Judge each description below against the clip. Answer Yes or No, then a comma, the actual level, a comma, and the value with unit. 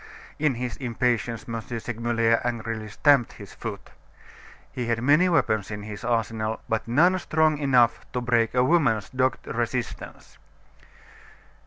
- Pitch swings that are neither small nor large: No, narrow, 2.3 semitones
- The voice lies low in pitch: Yes, low, 120 Hz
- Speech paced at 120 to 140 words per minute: Yes, slow, 135 wpm